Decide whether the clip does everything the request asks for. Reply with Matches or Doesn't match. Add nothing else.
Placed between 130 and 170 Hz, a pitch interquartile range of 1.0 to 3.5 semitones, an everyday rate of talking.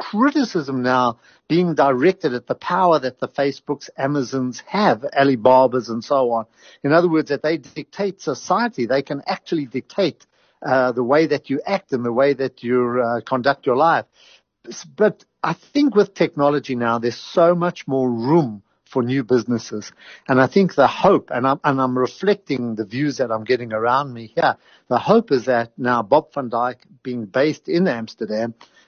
Doesn't match